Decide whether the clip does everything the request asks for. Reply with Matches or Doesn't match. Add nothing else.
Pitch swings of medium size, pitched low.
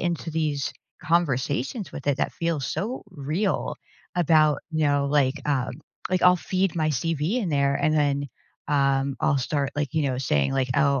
Doesn't match